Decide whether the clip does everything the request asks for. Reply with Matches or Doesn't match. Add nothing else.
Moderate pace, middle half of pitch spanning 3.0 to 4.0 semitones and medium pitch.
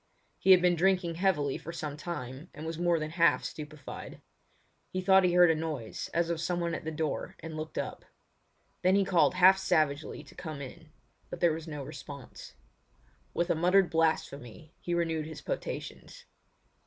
Doesn't match